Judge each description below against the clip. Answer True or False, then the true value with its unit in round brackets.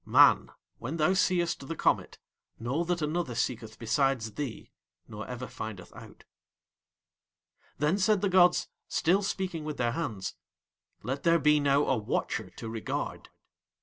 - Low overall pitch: False (145 Hz)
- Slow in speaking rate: False (145 wpm)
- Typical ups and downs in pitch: False (6.6 semitones)